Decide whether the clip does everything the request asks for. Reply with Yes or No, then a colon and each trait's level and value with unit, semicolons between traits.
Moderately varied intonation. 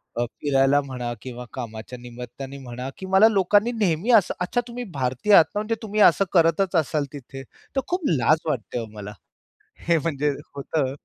No: wide, 7.4 semitones